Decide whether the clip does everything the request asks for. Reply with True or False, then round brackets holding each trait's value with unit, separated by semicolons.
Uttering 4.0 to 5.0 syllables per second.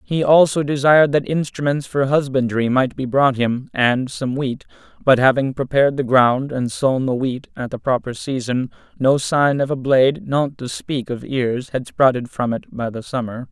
True (4.7 syllables/s)